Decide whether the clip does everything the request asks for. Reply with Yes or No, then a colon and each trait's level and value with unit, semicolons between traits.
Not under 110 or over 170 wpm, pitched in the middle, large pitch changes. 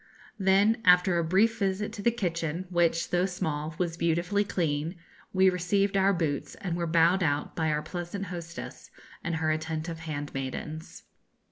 No: average, 155 wpm; medium, 170 Hz; average, 3.0 semitones